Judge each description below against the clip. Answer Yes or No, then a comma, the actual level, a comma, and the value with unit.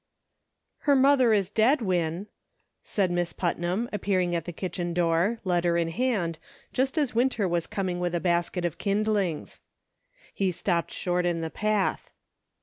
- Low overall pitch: No, medium, 180 Hz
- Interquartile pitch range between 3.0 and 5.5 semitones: Yes, average, 3.7 semitones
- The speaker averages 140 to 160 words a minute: Yes, average, 150 wpm